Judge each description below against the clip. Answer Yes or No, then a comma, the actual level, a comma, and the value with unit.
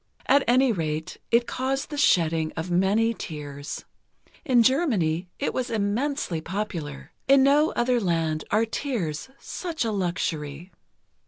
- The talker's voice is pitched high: Yes, high, 205 Hz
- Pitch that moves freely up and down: Yes, wide, 8.1 semitones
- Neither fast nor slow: No, slow, 130 wpm